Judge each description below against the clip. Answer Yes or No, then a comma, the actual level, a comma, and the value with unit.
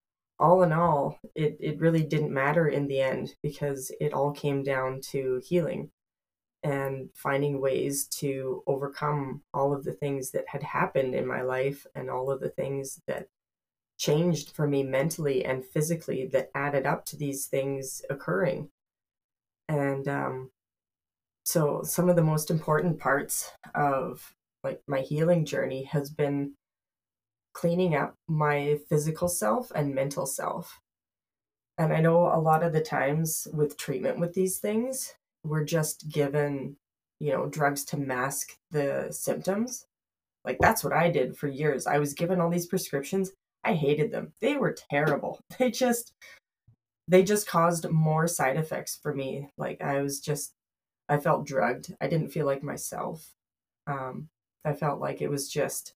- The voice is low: No, medium, 145 Hz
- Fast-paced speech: No, average, 160 wpm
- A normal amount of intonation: Yes, average, 3.4 semitones